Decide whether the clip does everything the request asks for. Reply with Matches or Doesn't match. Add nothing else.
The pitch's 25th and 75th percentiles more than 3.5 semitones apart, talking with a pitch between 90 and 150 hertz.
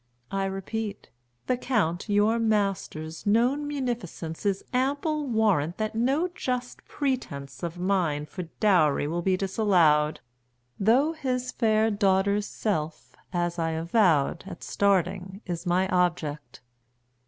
Doesn't match